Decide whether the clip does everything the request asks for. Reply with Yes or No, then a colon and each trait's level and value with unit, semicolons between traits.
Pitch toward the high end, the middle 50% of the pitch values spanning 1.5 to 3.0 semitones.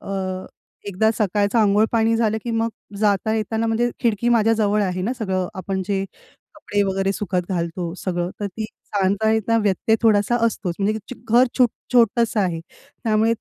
Yes: high, 210 Hz; narrow, 2.6 semitones